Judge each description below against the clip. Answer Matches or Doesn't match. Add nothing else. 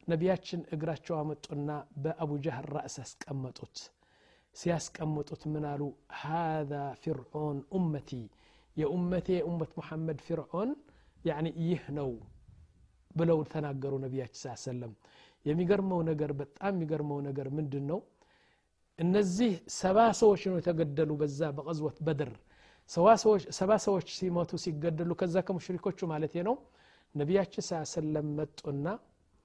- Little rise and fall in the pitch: Doesn't match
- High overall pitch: Doesn't match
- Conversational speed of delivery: Doesn't match